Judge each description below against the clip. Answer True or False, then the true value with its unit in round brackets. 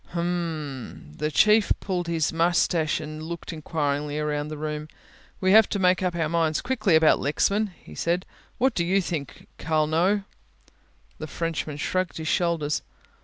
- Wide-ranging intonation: False (3.0 semitones)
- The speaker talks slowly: False (165 wpm)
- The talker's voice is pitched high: False (165 Hz)